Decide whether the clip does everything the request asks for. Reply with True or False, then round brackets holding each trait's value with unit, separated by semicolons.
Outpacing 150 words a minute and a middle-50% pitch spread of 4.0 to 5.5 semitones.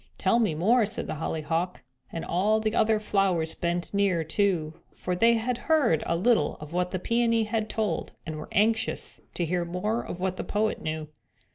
True (190 wpm; 4.7 semitones)